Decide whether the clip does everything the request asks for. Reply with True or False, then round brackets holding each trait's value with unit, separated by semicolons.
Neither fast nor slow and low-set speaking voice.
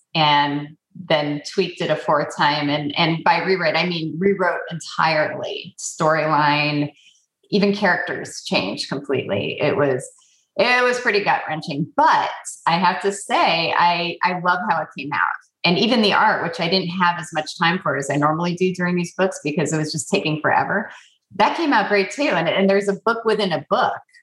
False (190 wpm; 175 Hz)